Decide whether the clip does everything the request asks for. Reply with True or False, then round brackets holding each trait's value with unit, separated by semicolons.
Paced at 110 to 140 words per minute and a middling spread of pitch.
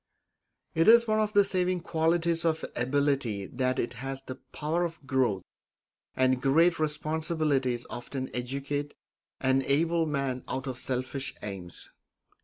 True (135 wpm; 4.2 semitones)